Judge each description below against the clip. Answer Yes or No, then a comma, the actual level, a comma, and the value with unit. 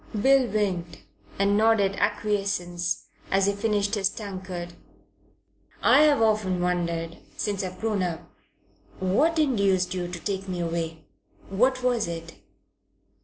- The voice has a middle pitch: No, high, 195 Hz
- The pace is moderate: No, slow, 120 wpm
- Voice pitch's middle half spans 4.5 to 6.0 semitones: No, average, 3.3 semitones